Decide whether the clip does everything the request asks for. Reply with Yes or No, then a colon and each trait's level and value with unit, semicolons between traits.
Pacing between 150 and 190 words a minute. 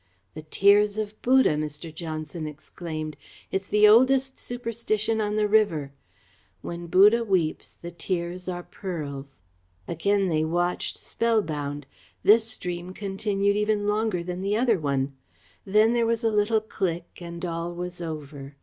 No: average, 140 wpm